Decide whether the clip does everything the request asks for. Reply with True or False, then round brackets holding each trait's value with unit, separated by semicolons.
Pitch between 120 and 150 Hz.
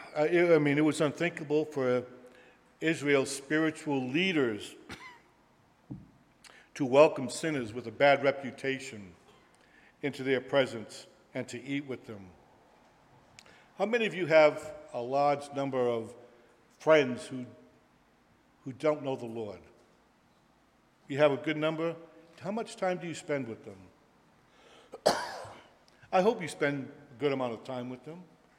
True (140 Hz)